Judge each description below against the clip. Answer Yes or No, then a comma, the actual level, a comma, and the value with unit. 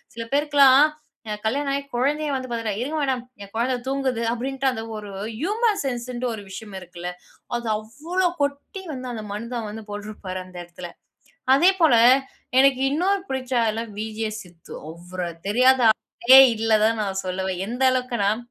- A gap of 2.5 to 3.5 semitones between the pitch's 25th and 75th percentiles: No, average, 4.3 semitones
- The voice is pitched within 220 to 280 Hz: Yes, high, 240 Hz